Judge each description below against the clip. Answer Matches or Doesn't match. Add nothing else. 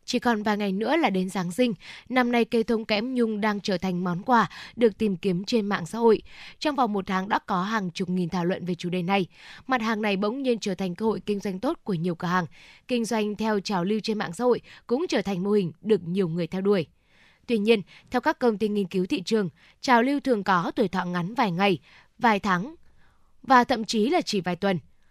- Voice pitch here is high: Matches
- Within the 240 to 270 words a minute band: Matches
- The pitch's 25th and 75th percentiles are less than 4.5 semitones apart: Matches